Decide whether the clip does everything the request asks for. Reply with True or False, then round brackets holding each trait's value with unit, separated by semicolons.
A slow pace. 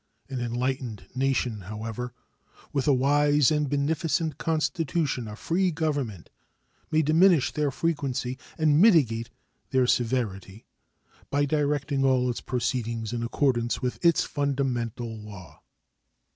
True (115 wpm)